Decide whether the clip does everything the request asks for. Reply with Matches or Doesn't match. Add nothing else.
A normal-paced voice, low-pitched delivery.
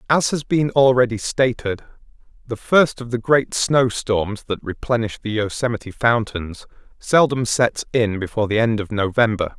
Matches